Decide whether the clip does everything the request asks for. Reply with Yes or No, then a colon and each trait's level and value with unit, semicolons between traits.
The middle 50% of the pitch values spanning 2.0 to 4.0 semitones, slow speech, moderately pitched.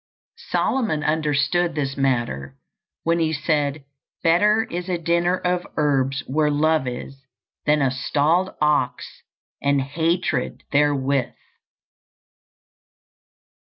Yes: average, 3.5 semitones; slow, 100 wpm; medium, 150 Hz